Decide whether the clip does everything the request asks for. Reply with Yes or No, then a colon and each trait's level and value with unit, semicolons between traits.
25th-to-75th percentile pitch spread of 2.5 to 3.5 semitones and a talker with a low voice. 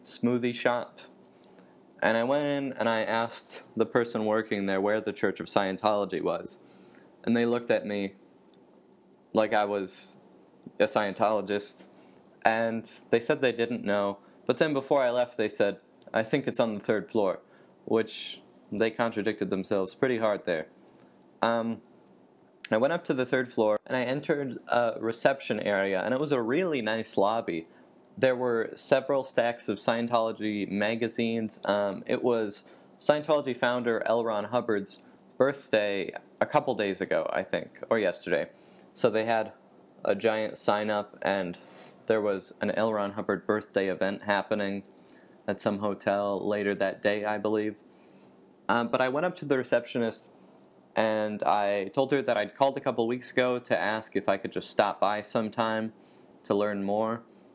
Yes: average, 2.9 semitones; low, 110 Hz